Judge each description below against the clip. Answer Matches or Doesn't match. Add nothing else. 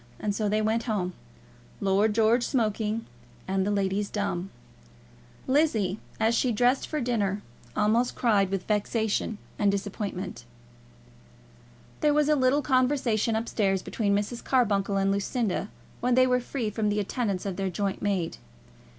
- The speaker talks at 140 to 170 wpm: Matches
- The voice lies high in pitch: Matches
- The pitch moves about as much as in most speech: Matches